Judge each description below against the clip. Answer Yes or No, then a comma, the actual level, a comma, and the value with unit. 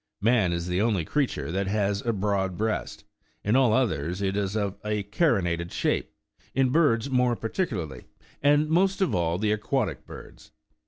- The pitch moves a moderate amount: Yes, average, 4.9 semitones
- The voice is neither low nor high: No, low, 105 Hz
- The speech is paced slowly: No, average, 165 wpm